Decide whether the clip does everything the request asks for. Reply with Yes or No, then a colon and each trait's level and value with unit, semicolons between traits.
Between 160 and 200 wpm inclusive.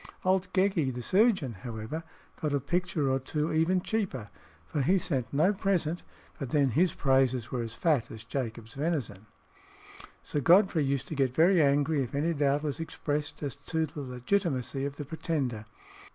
Yes: average, 170 wpm